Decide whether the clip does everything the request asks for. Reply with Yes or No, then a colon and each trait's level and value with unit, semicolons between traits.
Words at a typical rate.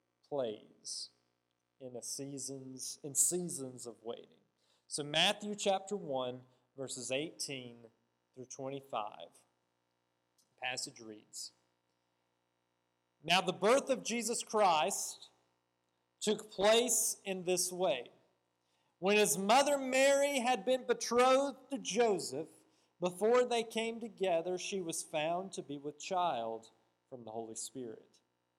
No: slow, 110 wpm